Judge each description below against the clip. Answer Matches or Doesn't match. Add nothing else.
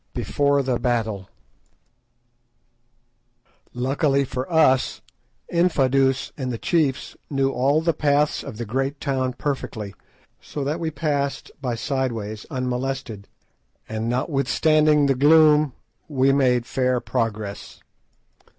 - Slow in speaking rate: Matches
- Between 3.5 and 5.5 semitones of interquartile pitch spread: Doesn't match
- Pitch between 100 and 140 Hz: Matches